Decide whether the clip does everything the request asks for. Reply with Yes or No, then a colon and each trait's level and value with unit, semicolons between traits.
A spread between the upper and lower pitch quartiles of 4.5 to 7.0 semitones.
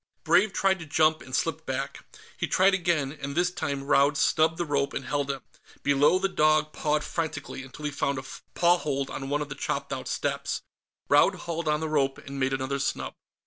No: average, 2.8 semitones